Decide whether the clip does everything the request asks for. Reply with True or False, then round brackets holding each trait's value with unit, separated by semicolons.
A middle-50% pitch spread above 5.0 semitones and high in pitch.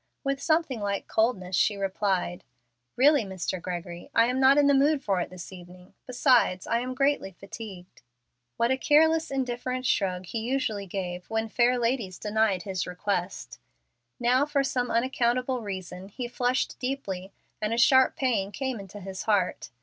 True (5.4 semitones; 225 Hz)